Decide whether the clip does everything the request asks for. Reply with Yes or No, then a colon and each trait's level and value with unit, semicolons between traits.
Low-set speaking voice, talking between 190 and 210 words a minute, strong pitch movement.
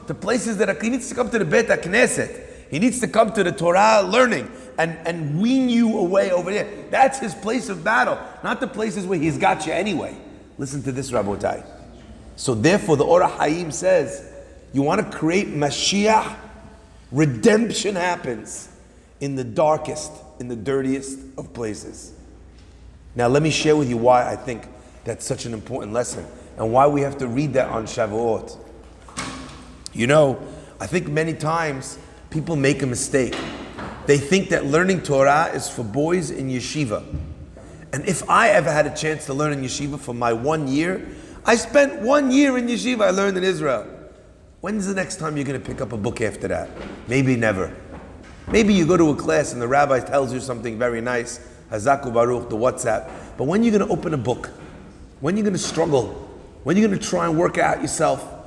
No: medium, 145 Hz; average, 195 wpm; wide, 7.4 semitones